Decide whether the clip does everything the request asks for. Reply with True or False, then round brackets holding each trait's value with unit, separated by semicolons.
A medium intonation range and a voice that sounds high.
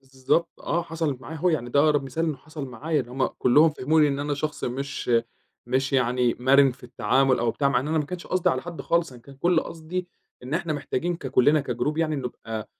False (3.7 semitones; 140 Hz)